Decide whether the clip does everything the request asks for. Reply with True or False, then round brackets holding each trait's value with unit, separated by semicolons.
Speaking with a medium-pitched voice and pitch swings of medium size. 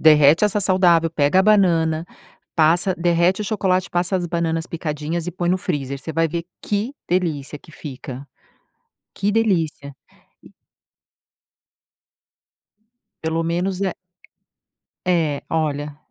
True (170 Hz; 3.0 semitones)